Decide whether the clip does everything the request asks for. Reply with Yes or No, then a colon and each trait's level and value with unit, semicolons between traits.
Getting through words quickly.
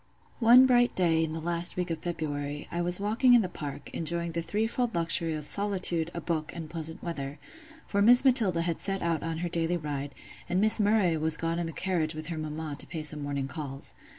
Yes: fast, 220 wpm